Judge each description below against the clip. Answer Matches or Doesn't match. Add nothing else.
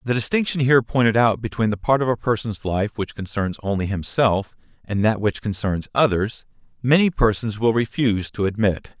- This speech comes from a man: Matches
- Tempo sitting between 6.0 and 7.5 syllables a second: Doesn't match